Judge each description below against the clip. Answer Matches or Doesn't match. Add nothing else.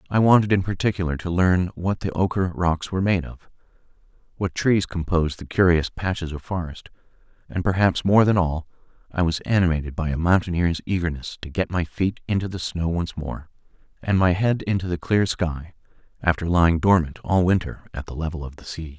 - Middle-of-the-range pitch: Doesn't match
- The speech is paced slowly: Doesn't match